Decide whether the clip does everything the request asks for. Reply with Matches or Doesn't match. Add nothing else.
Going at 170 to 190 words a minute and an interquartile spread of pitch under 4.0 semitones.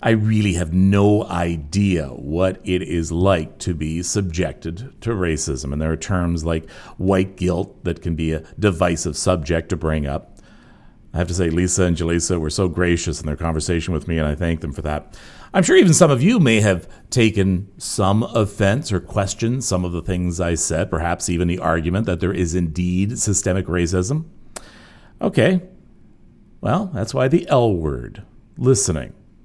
Matches